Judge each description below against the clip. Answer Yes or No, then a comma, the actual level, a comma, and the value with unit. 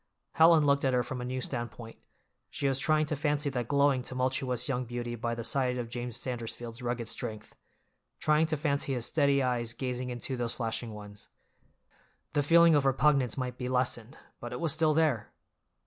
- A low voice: Yes, low, 125 Hz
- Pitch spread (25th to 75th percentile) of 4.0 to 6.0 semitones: No, average, 2.9 semitones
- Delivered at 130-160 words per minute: No, average, 180 wpm